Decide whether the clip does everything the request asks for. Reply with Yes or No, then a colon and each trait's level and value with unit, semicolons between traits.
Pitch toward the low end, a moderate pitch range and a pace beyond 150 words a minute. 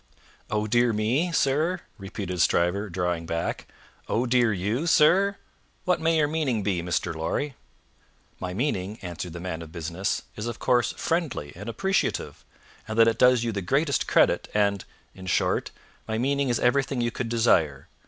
No: low, 110 Hz; wide, 7.0 semitones; average, 165 wpm